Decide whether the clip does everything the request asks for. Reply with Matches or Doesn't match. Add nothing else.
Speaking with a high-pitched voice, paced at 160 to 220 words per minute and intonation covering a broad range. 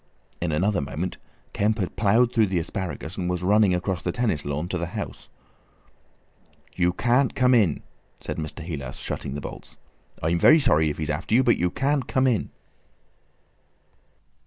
Doesn't match